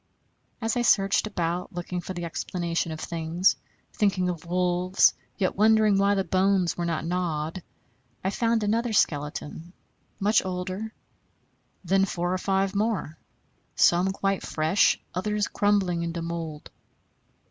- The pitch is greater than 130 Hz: Yes, medium, 185 Hz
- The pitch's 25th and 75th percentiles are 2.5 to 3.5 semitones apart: Yes, average, 2.8 semitones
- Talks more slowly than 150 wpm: Yes, slow, 135 wpm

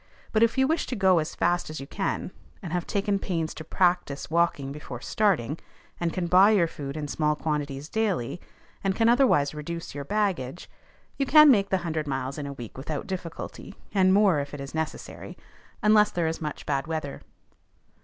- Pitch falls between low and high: Yes, medium, 165 Hz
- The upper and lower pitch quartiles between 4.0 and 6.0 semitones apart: Yes, average, 5.2 semitones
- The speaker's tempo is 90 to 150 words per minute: No, average, 195 wpm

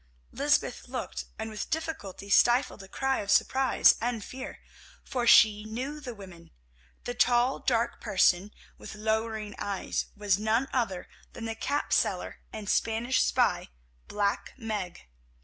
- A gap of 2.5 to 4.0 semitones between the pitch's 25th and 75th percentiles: Yes, average, 3.3 semitones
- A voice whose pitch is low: No, high, 220 Hz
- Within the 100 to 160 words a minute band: Yes, average, 140 wpm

